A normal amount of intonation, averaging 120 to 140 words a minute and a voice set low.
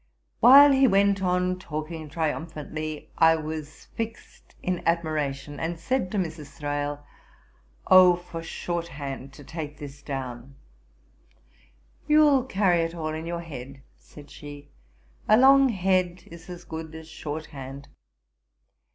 No: average, 3.9 semitones; slow, 135 wpm; medium, 160 Hz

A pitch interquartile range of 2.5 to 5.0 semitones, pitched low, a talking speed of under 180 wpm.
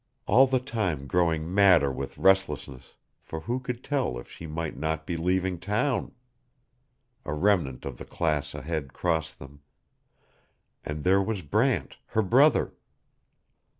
No: wide, 5.4 semitones; very low, 85 Hz; average, 140 wpm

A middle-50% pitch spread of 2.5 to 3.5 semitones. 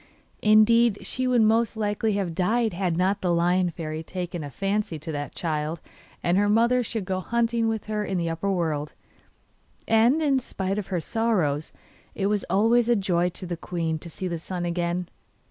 No: average, 4.5 semitones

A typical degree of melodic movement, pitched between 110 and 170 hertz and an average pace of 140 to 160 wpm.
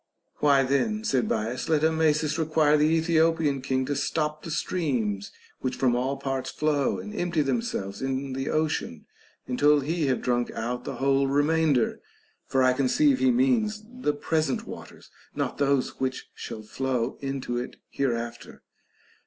Yes: average, 3.6 semitones; medium, 140 Hz; average, 155 wpm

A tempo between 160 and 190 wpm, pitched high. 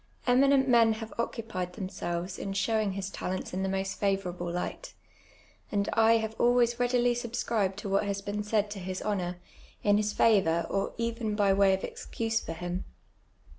Yes: average, 170 wpm; high, 205 Hz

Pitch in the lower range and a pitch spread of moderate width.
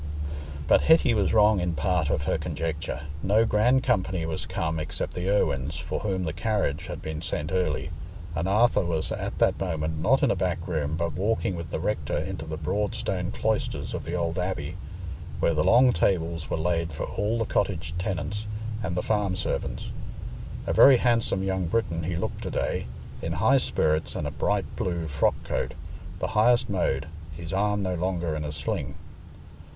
Yes: very low, 90 Hz; average, 4.1 semitones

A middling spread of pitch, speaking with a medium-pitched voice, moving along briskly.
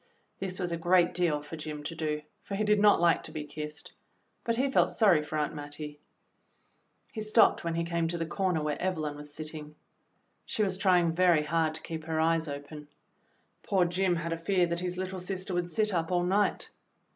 Yes: average, 3.1 semitones; medium, 170 Hz; fast, 225 wpm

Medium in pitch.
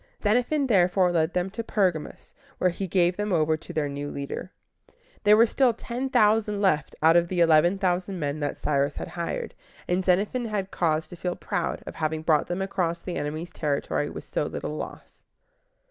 Yes: medium, 180 Hz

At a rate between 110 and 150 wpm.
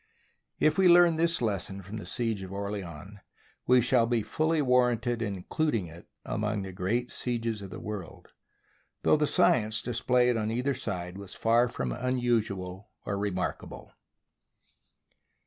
Yes: average, 145 wpm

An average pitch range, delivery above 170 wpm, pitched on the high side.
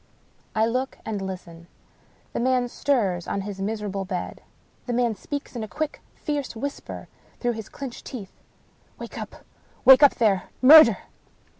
No: average, 4.9 semitones; average, 155 wpm; high, 230 Hz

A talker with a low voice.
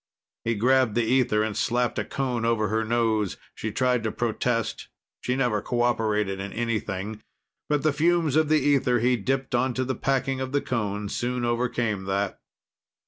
Yes: low, 120 Hz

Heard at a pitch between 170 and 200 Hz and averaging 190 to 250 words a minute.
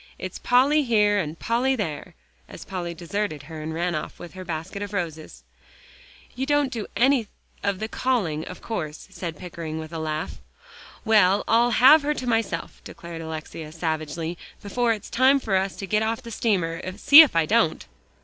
No: high, 190 Hz; average, 180 wpm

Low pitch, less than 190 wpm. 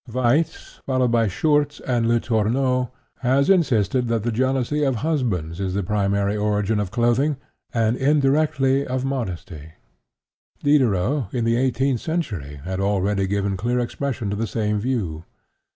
Yes: low, 120 Hz; average, 140 wpm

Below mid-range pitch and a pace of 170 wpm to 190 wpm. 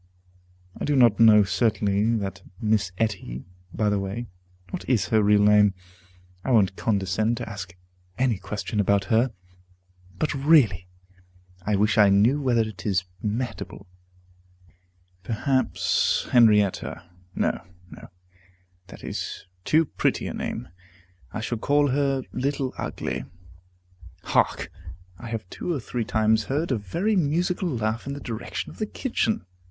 No: low, 110 Hz; average, 140 wpm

